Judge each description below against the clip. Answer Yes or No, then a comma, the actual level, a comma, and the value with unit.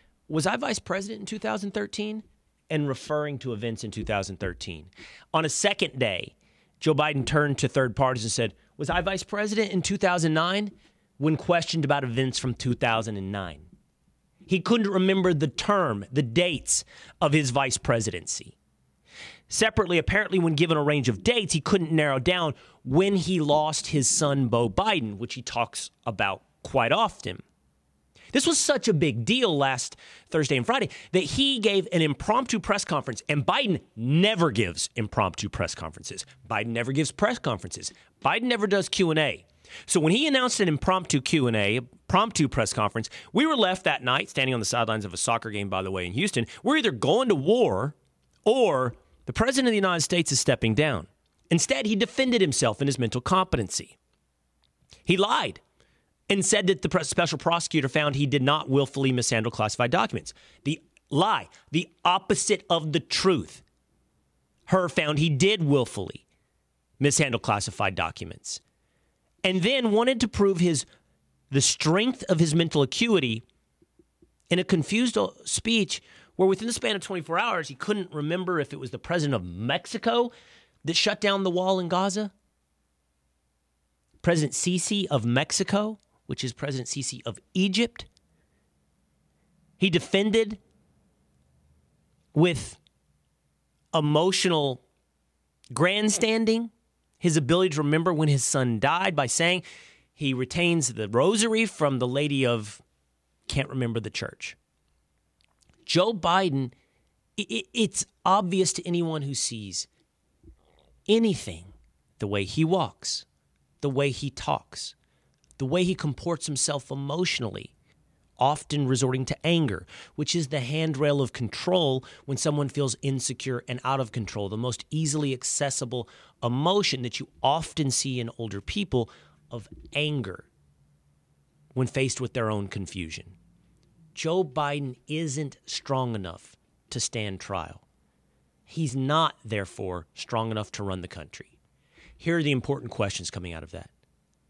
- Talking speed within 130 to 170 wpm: Yes, average, 145 wpm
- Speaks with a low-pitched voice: No, medium, 145 Hz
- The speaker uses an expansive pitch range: Yes, wide, 7.9 semitones